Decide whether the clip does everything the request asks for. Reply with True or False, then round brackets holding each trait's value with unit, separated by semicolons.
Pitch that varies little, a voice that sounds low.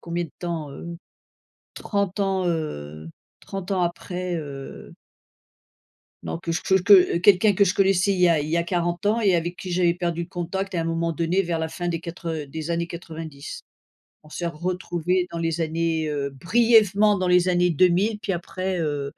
False (2.1 semitones; 175 Hz)